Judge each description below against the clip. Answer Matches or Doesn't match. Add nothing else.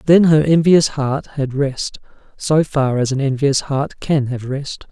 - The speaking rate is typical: Matches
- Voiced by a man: Matches